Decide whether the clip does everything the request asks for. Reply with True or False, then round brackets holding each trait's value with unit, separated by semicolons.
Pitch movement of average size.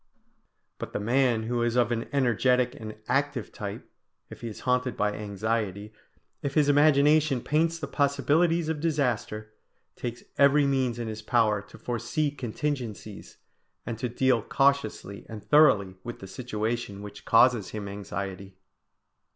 True (4.7 semitones)